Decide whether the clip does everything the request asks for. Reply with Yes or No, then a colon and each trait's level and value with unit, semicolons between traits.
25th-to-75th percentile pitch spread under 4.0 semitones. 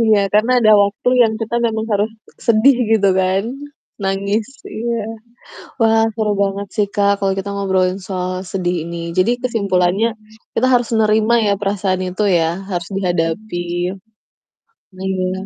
Yes: average, 2.8 semitones